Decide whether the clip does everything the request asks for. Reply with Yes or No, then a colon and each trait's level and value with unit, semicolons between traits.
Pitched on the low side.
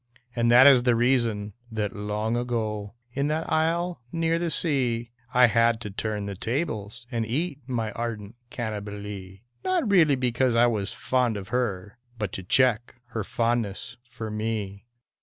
Yes: low, 115 Hz